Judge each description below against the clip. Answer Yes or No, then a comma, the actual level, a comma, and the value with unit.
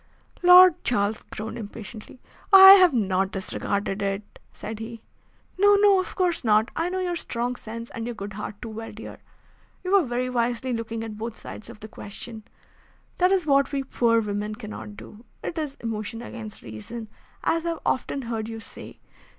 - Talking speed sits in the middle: Yes, average, 185 wpm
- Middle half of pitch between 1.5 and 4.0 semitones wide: No, average, 5.0 semitones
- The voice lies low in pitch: No, high, 230 Hz